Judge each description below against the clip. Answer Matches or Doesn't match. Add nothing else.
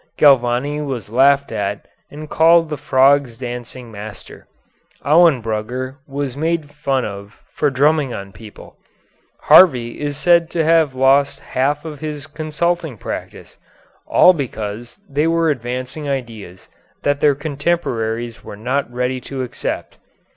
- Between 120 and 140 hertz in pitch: Matches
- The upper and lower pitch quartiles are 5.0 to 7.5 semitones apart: Doesn't match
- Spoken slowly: Matches